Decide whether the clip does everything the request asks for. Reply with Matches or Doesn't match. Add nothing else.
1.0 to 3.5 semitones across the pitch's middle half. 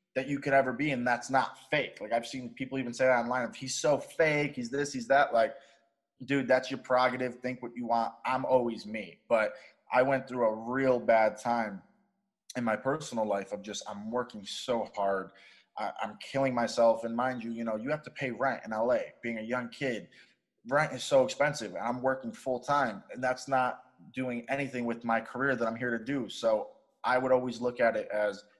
Matches